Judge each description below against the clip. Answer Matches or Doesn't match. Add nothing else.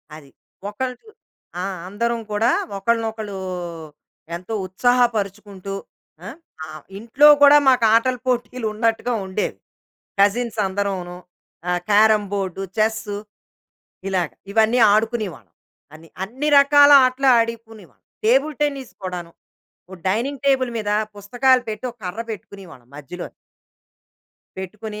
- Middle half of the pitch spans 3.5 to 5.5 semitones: Matches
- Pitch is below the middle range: Doesn't match